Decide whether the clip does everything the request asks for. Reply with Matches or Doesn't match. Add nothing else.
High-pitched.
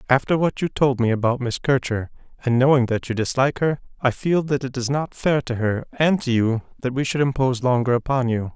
Doesn't match